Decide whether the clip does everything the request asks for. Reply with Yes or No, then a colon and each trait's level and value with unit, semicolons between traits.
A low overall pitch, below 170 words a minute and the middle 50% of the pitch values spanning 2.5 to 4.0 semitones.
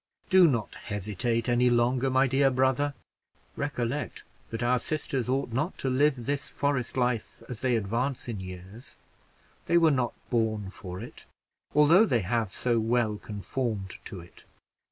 Yes: low, 120 Hz; average, 155 wpm; average, 3.4 semitones